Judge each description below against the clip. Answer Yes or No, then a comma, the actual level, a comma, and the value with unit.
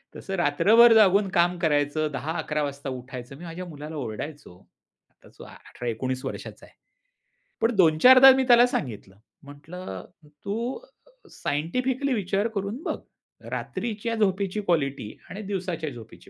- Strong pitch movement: Yes, wide, 6.5 semitones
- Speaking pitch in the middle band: Yes, medium, 170 Hz